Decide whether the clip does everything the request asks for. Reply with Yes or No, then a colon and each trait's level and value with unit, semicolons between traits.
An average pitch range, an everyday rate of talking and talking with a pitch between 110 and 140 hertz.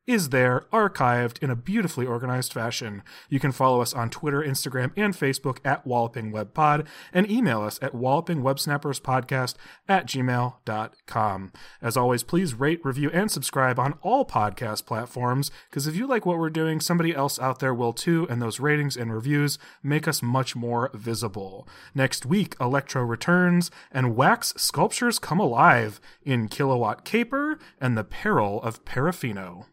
Yes: average, 4.8 semitones; average, 155 wpm; low, 135 Hz